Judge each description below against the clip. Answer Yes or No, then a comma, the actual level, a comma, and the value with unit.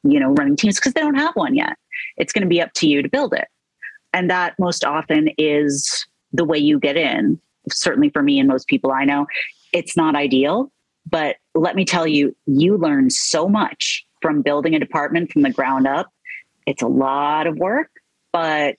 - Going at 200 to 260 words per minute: Yes, fast, 205 wpm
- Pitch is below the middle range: No, medium, 170 Hz